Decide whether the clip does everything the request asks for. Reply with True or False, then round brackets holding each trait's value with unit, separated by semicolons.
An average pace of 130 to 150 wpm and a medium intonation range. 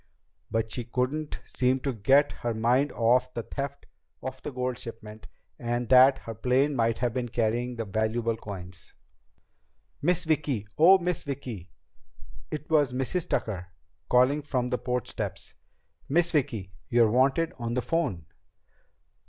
True (145 wpm; 3.6 semitones)